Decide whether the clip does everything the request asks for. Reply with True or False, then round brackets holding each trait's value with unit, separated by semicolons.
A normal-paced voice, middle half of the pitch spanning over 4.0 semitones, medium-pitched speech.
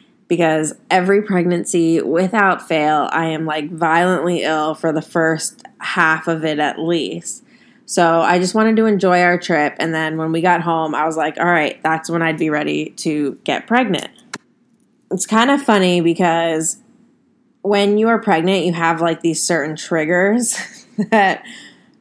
True (165 wpm; 4.6 semitones; 175 Hz)